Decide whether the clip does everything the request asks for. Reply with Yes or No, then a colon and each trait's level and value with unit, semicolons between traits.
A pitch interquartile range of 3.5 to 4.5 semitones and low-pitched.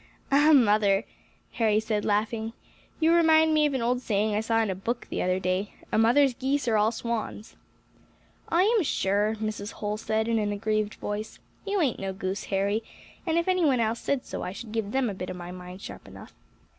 No: average, 4.2 semitones; high, 220 Hz